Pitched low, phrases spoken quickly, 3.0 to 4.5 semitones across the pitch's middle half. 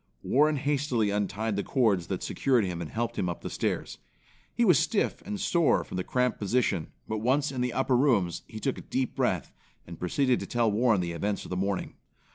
No: low, 115 Hz; fast, 215 wpm; average, 5.2 semitones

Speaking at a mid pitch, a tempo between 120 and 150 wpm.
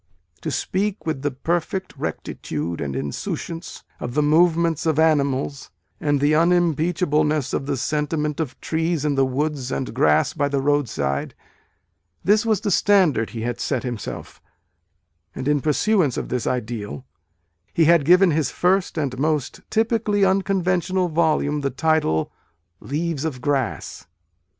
Yes: medium, 150 Hz; average, 140 wpm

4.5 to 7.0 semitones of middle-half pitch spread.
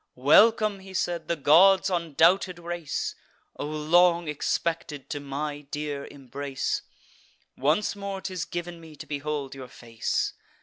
No: average, 3.6 semitones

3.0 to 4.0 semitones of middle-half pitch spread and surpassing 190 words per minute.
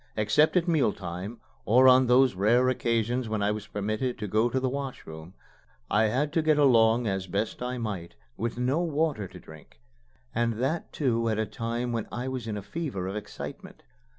Yes: average, 3.6 semitones; average, 200 wpm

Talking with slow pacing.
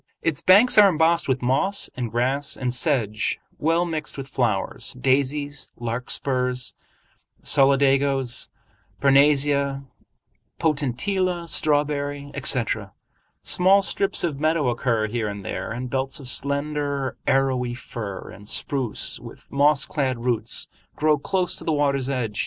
Yes: slow, 125 wpm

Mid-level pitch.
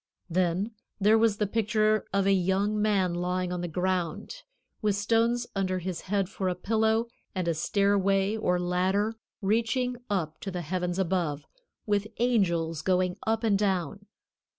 No: high, 195 Hz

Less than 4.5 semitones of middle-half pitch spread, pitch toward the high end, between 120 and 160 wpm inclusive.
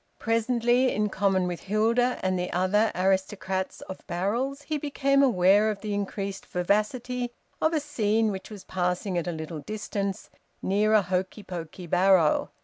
Yes: average, 3.5 semitones; high, 200 Hz; average, 155 wpm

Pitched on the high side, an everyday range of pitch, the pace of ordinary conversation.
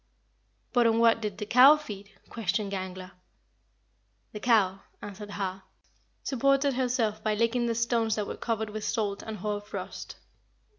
No: high, 215 Hz; narrow, 2.3 semitones; average, 150 wpm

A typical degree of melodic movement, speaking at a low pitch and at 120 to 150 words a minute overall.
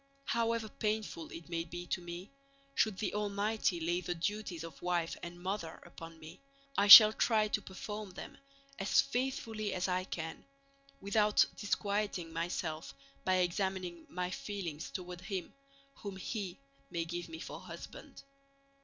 No: average, 3.3 semitones; medium, 185 Hz; average, 145 wpm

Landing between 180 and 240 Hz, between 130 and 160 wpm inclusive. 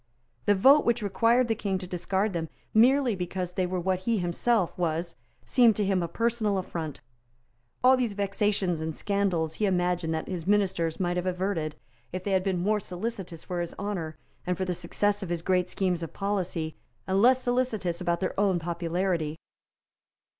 No: medium, 185 Hz; average, 180 wpm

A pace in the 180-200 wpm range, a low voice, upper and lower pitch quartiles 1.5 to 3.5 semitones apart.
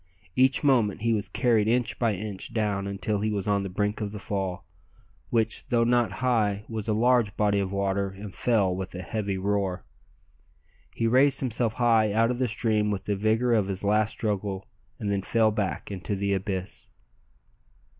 Yes: average, 185 wpm; low, 105 Hz; narrow, 2.6 semitones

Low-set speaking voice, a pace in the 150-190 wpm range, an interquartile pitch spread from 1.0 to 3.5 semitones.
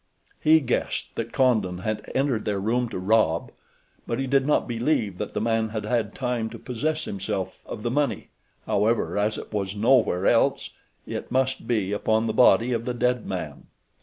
Yes: low, 115 Hz; average, 185 wpm; average, 3.1 semitones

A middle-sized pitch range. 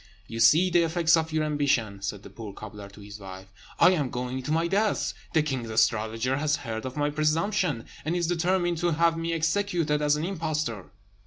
No: wide, 6.5 semitones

